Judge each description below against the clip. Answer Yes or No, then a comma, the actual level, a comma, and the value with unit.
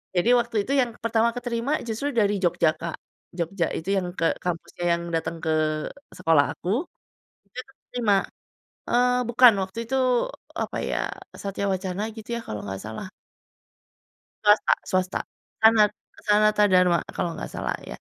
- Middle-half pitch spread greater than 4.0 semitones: Yes, average, 4.6 semitones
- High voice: Yes, high, 200 Hz